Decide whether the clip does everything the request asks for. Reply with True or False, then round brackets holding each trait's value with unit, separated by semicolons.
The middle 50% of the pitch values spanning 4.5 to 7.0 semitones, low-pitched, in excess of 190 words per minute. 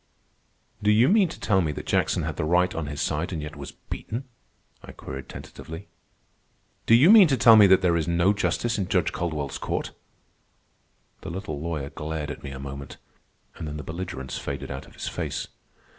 True (5.2 semitones; 85 Hz; 200 wpm)